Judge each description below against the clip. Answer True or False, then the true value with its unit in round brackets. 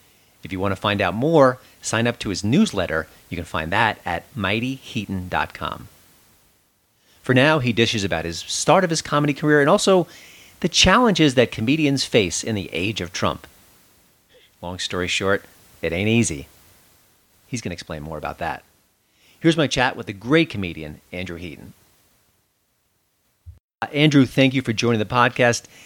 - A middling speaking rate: True (165 wpm)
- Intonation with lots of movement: True (6.6 semitones)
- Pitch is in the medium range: False (110 Hz)